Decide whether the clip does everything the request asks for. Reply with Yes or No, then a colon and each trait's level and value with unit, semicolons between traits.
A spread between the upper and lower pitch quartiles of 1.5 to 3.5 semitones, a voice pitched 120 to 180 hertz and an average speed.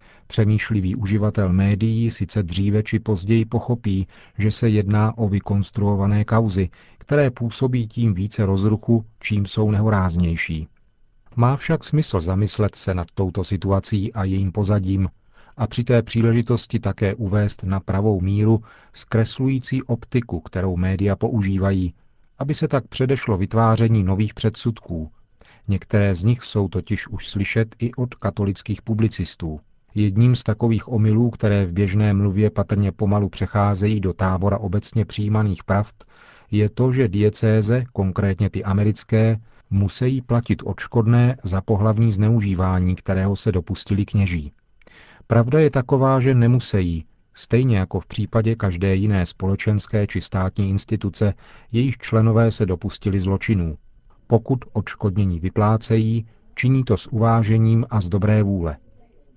No: narrow, 2.6 semitones; low, 105 Hz; average, 130 wpm